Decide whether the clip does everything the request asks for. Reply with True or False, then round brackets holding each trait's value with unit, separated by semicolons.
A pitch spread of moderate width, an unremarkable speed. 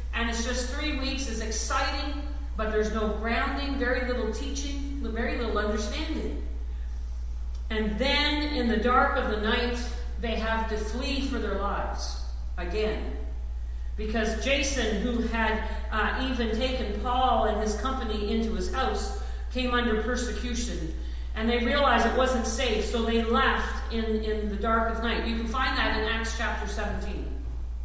True (3.0 semitones; 155 wpm)